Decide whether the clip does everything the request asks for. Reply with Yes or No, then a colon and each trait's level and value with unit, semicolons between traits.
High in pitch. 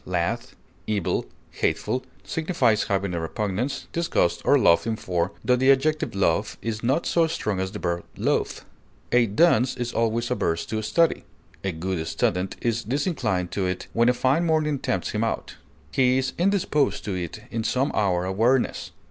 No: low, 110 Hz